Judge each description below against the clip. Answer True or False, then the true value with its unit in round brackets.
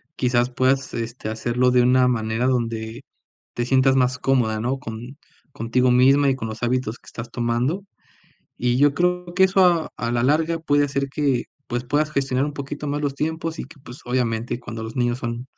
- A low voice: True (125 Hz)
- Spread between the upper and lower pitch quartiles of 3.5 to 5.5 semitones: False (3.1 semitones)